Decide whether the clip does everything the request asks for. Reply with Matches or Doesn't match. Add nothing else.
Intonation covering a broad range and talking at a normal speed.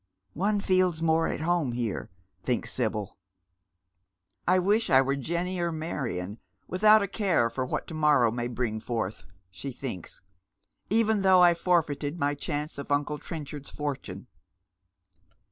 Matches